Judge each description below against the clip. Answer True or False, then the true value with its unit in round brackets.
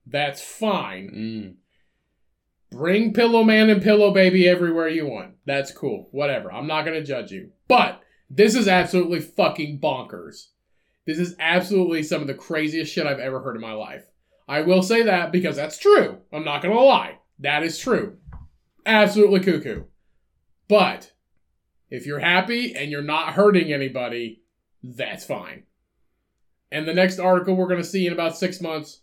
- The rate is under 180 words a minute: True (165 wpm)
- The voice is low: False (160 Hz)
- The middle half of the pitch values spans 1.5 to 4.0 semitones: False (5.5 semitones)